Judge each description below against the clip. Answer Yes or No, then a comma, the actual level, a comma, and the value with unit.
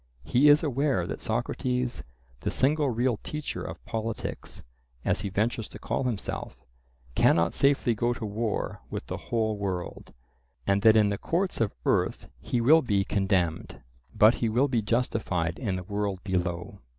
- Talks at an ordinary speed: Yes, average, 165 wpm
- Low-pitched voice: Yes, low, 110 Hz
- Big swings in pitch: No, average, 4.3 semitones